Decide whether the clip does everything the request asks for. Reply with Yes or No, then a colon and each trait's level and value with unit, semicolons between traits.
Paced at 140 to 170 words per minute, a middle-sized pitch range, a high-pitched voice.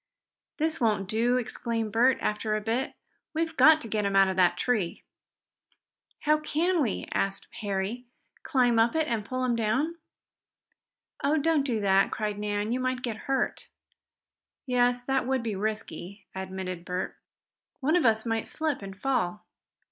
Yes: average, 160 wpm; average, 4.4 semitones; high, 230 Hz